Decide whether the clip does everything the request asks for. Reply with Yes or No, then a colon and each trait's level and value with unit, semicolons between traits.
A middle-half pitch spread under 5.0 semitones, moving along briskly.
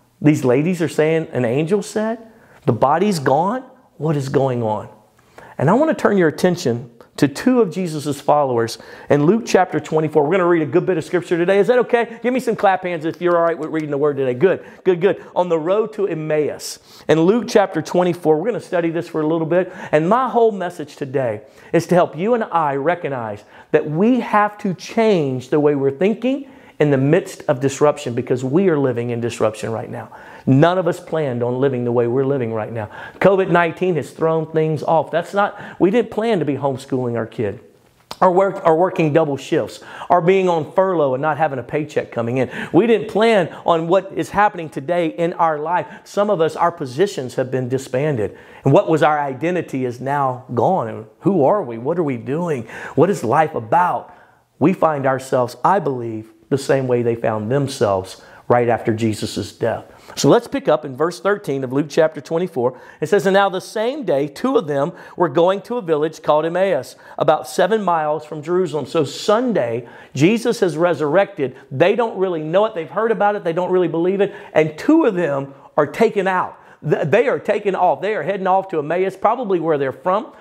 No: wide, 5.6 semitones; fast, 210 wpm